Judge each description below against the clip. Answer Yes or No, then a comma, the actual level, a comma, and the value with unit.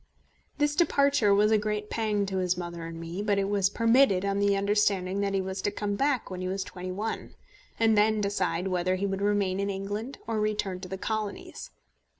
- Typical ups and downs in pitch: No, narrow, 2.1 semitones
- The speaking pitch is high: Yes, high, 200 Hz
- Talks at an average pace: No, fast, 210 wpm